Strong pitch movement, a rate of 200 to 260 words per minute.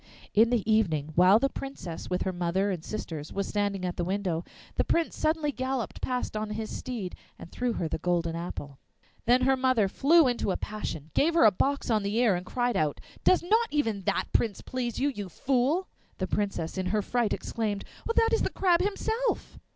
Yes: wide, 6.2 semitones; fast, 205 wpm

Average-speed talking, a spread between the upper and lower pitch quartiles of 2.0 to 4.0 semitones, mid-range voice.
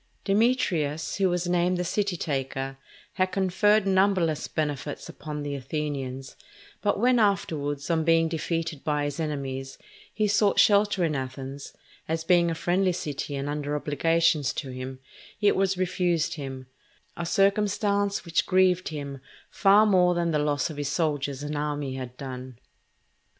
No: average, 150 wpm; average, 4.6 semitones; medium, 160 Hz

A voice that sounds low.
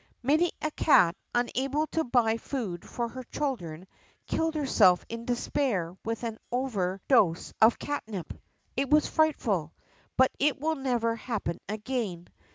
No: high, 240 Hz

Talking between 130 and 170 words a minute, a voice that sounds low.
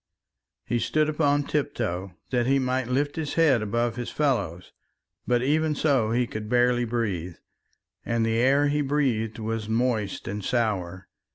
Yes: average, 155 wpm; low, 120 Hz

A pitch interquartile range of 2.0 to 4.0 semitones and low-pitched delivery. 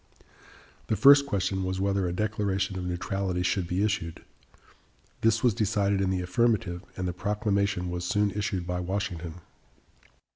Yes: narrow, 2.6 semitones; very low, 95 Hz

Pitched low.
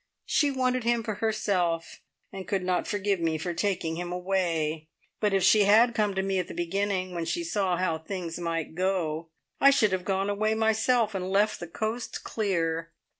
No: high, 190 Hz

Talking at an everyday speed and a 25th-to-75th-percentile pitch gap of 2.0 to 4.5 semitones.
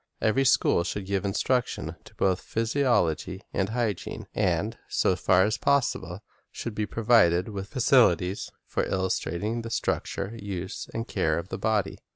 Yes: average, 155 wpm; average, 3.6 semitones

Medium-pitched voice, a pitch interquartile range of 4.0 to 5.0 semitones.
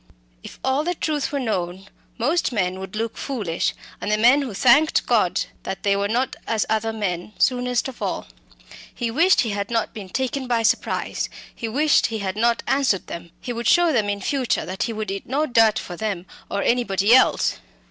No: high, 225 Hz; average, 4.5 semitones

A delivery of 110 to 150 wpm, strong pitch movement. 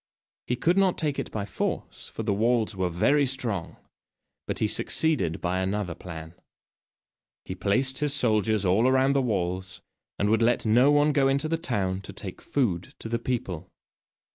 No: average, 175 wpm; wide, 6.2 semitones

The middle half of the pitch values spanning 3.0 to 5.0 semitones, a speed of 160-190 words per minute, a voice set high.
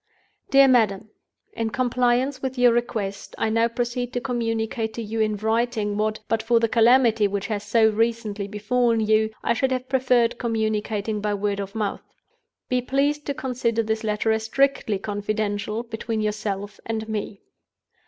No: narrow, 2.4 semitones; average, 165 wpm; high, 225 Hz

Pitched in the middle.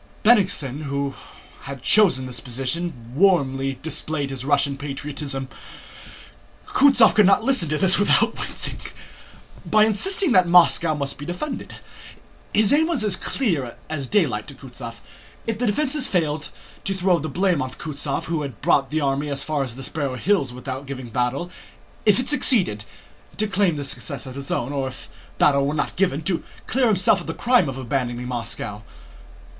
Yes: medium, 150 Hz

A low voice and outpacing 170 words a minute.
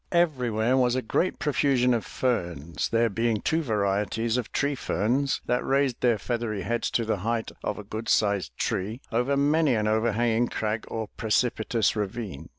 No: low, 115 Hz; average, 165 wpm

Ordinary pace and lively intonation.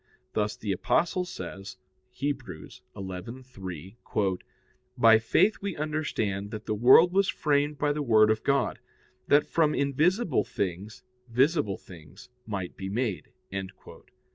No: slow, 120 wpm; wide, 7.0 semitones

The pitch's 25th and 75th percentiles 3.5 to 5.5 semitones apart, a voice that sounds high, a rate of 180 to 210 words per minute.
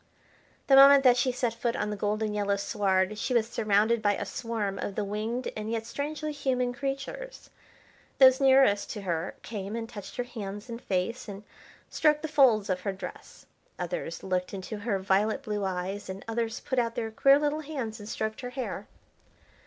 Yes: average, 4.0 semitones; high, 225 Hz; average, 190 wpm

